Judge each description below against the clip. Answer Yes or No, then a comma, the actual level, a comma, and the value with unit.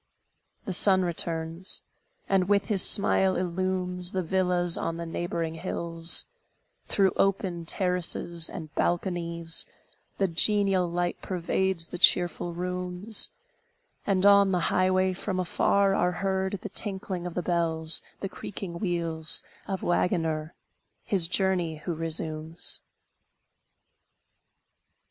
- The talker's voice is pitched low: No, medium, 180 Hz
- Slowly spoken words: Yes, slow, 115 wpm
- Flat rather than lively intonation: Yes, narrow, 2.1 semitones